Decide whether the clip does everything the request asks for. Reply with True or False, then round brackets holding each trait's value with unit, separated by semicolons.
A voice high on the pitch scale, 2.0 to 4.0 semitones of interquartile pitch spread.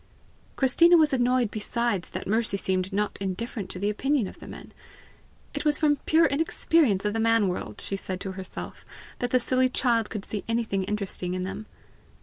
False (220 Hz; 4.7 semitones)